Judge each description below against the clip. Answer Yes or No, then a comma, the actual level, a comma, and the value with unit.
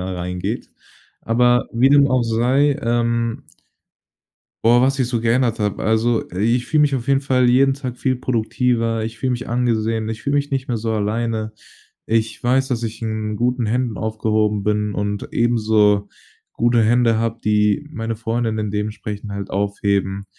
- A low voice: Yes, low, 115 Hz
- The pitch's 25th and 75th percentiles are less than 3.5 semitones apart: Yes, narrow, 2.4 semitones